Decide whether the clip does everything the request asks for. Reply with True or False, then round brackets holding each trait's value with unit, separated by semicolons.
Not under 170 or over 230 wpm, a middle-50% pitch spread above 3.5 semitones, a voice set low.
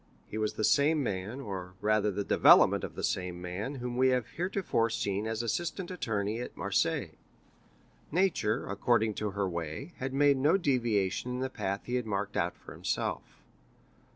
True (175 wpm; 4.8 semitones; 110 Hz)